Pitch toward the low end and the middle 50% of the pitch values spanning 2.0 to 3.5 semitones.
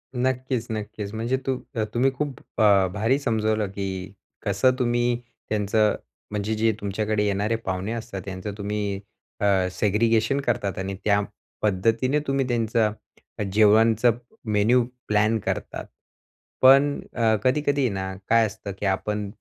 Yes: low, 110 Hz; average, 2.9 semitones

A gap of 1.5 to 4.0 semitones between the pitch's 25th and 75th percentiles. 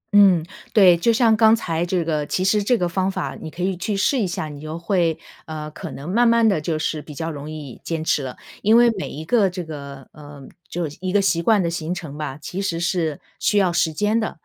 No: average, 4.4 semitones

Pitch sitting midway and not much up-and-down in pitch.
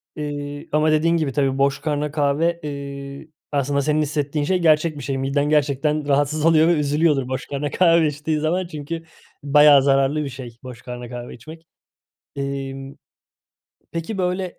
Yes: medium, 145 Hz; narrow, 2.2 semitones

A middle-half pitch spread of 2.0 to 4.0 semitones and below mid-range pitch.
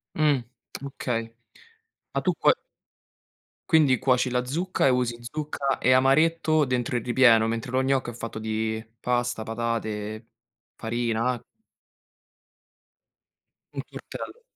Yes: average, 2.8 semitones; low, 125 Hz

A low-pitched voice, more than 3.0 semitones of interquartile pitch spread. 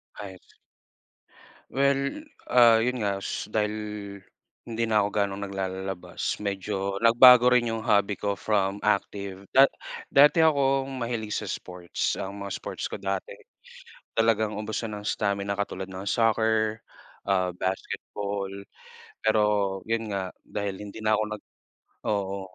No: low, 105 Hz; narrow, 2.6 semitones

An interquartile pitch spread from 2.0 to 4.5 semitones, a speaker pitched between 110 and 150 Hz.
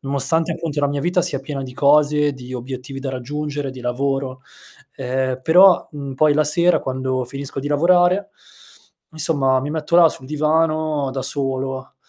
Yes: narrow, 2.6 semitones; medium, 140 Hz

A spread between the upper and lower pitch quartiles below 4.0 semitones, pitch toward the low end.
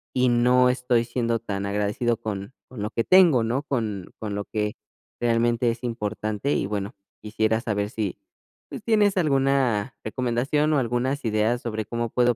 Yes: average, 2.9 semitones; low, 120 Hz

